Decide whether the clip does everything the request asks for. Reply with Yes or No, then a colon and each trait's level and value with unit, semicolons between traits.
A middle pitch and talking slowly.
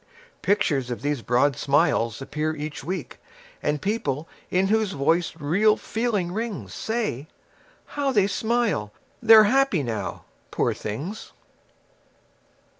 Yes: medium, 175 Hz; slow, 115 wpm